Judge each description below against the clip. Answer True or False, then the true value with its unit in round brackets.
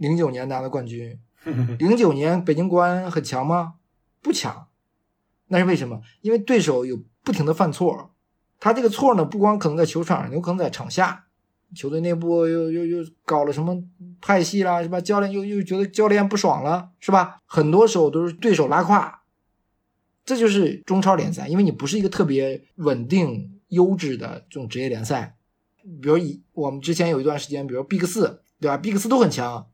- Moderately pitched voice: True (170 Hz)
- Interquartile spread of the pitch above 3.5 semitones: True (5.2 semitones)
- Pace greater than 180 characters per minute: True (295 characters per minute)